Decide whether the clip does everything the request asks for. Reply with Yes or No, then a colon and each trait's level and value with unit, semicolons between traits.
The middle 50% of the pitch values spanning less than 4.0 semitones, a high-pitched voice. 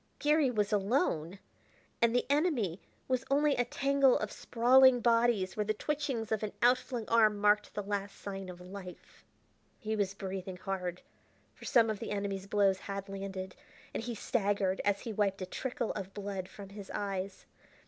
Yes: average, 3.6 semitones; high, 205 Hz